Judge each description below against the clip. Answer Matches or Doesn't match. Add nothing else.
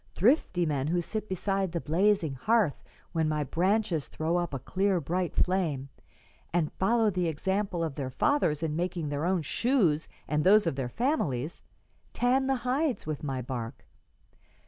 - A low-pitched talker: Doesn't match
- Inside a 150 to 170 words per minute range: Matches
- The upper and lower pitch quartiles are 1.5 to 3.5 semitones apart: Doesn't match